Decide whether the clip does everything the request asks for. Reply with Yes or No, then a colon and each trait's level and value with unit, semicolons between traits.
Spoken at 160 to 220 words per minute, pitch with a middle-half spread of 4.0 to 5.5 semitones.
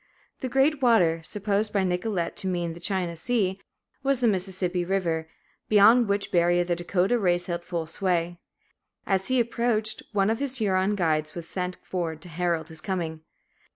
No: average, 170 wpm; average, 3.5 semitones